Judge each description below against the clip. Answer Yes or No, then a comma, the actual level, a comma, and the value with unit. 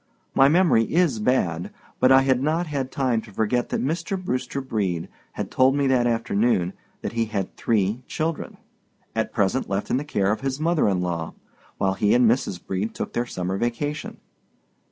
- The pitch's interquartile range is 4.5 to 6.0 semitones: Yes, average, 5.1 semitones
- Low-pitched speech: Yes, low, 120 Hz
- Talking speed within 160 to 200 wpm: Yes, average, 185 wpm